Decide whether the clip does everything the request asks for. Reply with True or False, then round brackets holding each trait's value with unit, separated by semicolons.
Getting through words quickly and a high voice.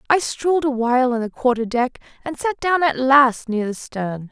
True (220 wpm; 260 Hz)